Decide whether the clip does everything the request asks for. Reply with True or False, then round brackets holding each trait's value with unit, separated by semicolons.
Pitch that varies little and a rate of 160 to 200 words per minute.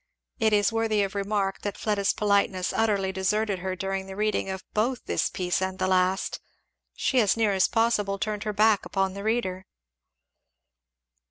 True (2.0 semitones; 170 wpm)